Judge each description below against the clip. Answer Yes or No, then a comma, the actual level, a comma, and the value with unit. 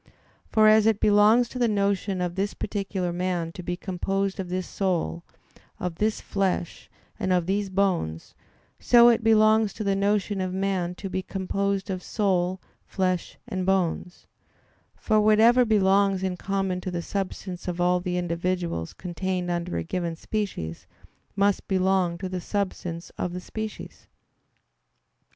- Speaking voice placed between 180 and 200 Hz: Yes, high, 190 Hz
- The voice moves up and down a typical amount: No, narrow, 2.1 semitones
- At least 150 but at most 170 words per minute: Yes, average, 155 wpm